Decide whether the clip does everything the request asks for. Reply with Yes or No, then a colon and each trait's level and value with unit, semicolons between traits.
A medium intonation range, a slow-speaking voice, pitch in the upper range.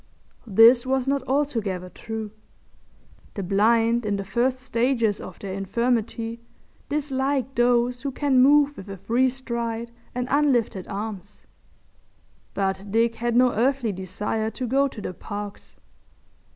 Yes: average, 4.0 semitones; slow, 130 wpm; high, 235 Hz